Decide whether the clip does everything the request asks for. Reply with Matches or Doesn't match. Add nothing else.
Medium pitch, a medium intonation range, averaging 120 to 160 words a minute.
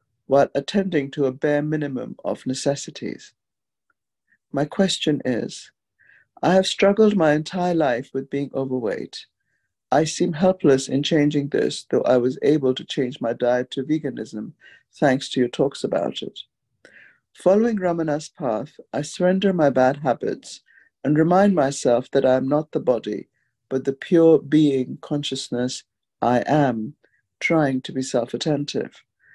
Matches